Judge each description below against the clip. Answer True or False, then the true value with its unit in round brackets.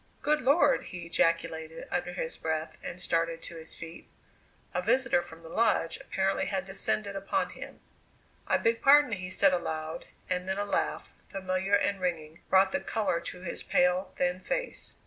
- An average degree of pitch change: True (3.2 semitones)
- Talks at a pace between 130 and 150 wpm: False (170 wpm)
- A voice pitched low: False (185 Hz)